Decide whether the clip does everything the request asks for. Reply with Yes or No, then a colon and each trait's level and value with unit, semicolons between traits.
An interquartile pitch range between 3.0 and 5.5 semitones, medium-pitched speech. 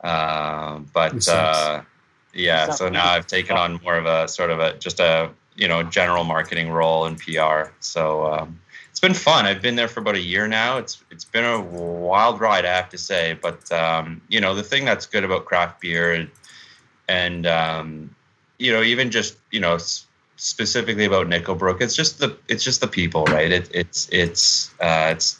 No: average, 4.6 semitones; very low, 85 Hz